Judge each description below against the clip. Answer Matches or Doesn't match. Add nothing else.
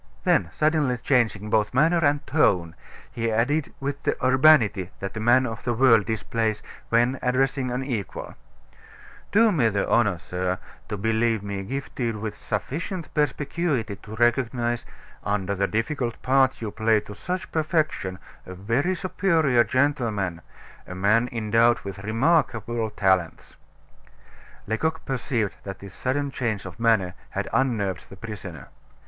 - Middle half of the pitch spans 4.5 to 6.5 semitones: Matches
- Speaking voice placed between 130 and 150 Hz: Doesn't match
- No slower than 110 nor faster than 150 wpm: Matches